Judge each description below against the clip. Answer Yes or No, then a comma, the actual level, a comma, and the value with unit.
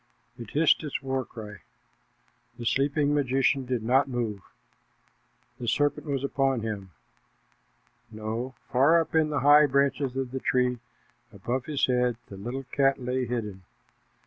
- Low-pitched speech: Yes, low, 130 Hz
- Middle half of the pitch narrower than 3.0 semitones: Yes, narrow, 2.6 semitones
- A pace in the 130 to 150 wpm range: Yes, average, 145 wpm